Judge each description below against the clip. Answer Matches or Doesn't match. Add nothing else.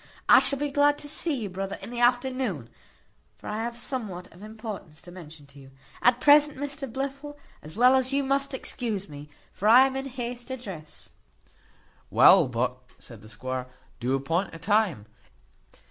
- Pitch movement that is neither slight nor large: Doesn't match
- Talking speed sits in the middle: Matches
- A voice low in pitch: Doesn't match